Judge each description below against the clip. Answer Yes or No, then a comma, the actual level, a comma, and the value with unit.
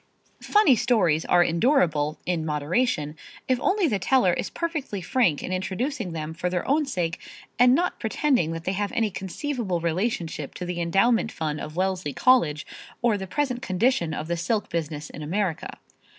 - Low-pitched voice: No, medium, 185 Hz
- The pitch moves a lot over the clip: Yes, wide, 6.9 semitones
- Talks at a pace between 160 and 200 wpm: Yes, average, 170 wpm